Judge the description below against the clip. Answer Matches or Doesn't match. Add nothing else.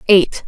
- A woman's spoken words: Matches